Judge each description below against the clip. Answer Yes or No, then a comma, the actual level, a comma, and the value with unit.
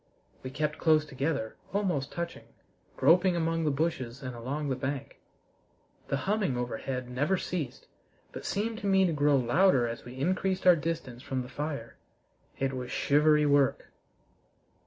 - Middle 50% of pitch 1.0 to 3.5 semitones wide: No, average, 4.6 semitones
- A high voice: No, medium, 145 Hz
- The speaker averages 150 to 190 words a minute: Yes, average, 155 wpm